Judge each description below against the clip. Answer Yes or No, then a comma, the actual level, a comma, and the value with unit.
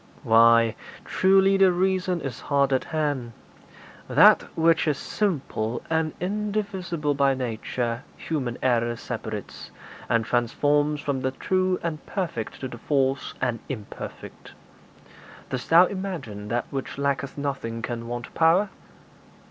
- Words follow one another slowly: Yes, slow, 125 wpm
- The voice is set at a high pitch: No, medium, 140 Hz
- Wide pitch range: Yes, wide, 6.1 semitones